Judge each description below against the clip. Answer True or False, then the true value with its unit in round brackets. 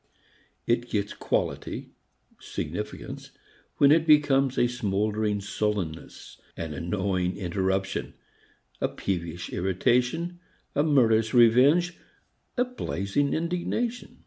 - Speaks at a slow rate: True (95 wpm)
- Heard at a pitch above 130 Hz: False (115 Hz)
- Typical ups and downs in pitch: False (7.2 semitones)